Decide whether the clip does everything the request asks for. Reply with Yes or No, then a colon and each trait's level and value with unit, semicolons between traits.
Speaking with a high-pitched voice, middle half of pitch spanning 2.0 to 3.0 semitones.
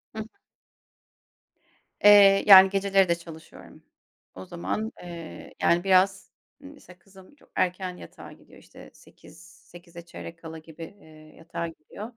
No: medium, 180 Hz; average, 2.7 semitones